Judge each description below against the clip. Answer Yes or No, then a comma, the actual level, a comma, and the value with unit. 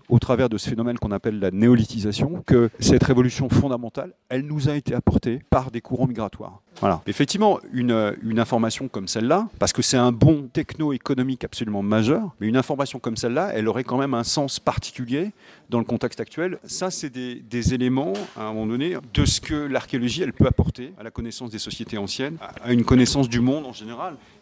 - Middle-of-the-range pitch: No, low, 125 Hz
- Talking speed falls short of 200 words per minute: No, average, 205 wpm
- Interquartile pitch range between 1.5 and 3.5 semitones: Yes, average, 3.1 semitones